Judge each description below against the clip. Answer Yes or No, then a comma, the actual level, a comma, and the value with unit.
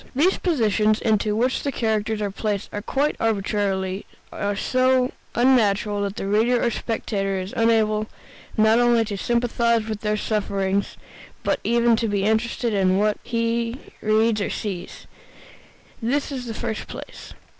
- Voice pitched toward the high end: Yes, high, 220 Hz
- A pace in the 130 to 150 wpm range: Yes, average, 145 wpm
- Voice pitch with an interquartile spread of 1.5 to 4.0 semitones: Yes, narrow, 2.5 semitones